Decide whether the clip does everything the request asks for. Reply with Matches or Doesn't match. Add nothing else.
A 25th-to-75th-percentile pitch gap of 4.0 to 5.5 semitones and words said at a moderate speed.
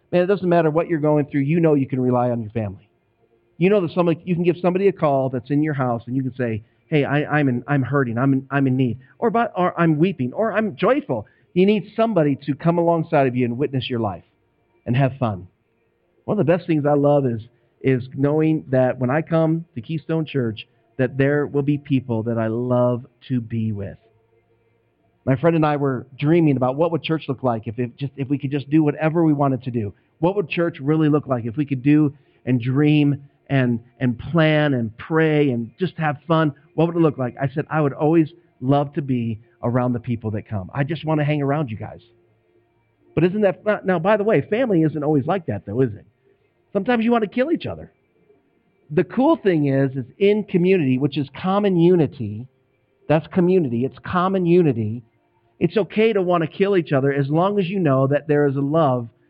Doesn't match